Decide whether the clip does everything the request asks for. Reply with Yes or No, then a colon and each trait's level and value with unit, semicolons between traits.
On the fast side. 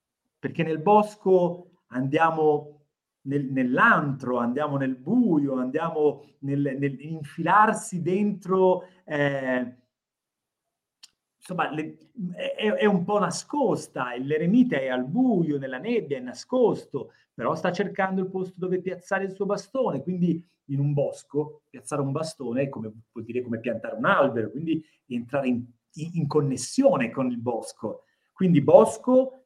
No: average, 130 wpm